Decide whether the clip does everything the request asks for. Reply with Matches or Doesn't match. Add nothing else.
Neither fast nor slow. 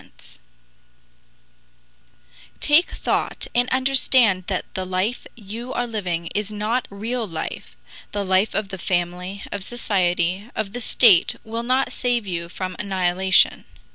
Doesn't match